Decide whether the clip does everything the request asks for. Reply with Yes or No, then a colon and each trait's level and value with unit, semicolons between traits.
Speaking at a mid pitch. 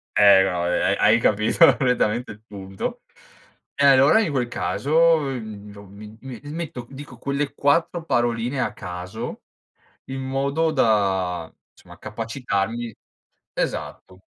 No: low, 120 Hz